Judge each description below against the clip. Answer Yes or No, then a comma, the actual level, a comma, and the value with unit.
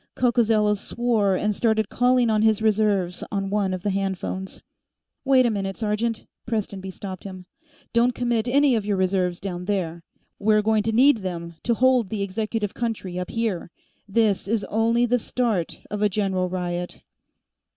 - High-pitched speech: Yes, high, 210 Hz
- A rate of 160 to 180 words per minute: Yes, average, 165 wpm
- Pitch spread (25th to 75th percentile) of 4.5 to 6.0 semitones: No, average, 3.2 semitones